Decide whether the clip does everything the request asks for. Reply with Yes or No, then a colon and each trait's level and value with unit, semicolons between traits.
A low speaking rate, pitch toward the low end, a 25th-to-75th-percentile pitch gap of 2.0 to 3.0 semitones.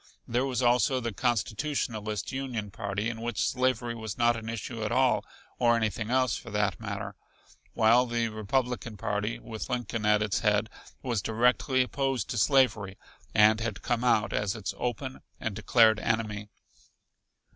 No: average, 155 wpm; low, 115 Hz; average, 2.7 semitones